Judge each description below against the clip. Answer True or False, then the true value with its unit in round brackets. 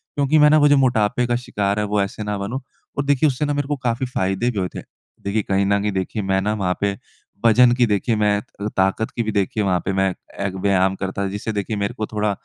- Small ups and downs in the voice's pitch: False (3.8 semitones)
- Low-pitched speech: True (105 Hz)